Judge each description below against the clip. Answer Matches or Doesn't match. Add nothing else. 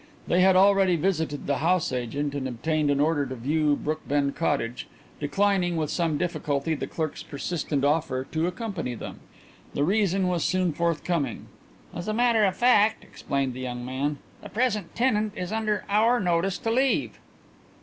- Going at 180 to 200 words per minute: Doesn't match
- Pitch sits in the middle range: Matches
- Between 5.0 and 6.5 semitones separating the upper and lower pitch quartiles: Matches